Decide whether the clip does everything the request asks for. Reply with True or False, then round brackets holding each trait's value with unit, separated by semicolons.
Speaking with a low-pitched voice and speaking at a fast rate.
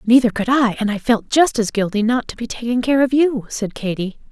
False (230 Hz; 250 wpm)